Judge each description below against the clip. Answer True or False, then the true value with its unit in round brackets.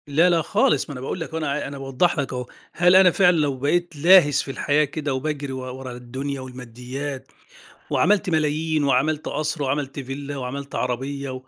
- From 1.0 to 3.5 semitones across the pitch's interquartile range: True (2.9 semitones)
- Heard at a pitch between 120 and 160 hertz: True (140 Hz)